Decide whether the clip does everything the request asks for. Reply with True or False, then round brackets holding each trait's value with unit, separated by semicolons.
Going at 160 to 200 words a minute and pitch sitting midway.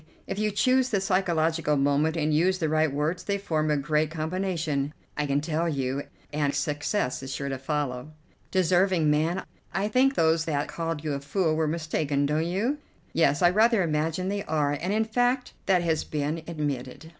True (185 wpm; 160 Hz)